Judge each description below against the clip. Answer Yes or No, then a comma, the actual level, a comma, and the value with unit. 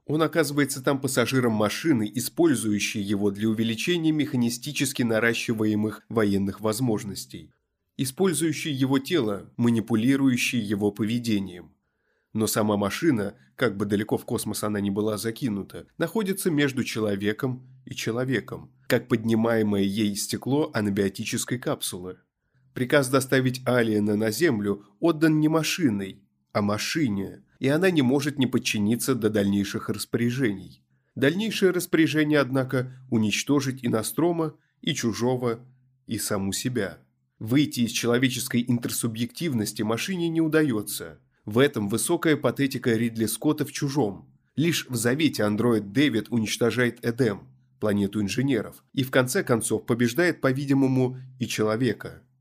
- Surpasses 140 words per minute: No, average, 120 wpm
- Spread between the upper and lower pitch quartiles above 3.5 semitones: Yes, average, 4.3 semitones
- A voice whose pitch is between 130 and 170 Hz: No, low, 120 Hz